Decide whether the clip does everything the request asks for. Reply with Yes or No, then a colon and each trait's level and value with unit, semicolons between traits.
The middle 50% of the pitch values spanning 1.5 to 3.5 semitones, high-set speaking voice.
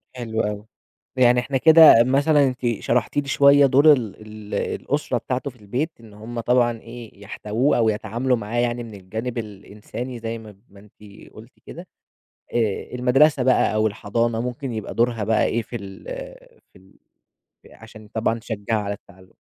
No: average, 2.8 semitones; low, 115 Hz